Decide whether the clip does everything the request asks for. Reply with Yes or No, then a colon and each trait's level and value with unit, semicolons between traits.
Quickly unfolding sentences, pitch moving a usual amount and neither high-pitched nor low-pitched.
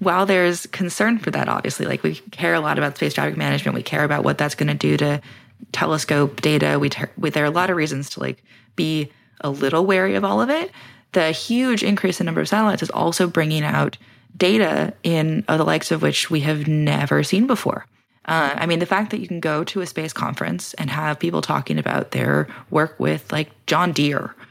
No: fast, 225 wpm; wide, 6.2 semitones; medium, 155 Hz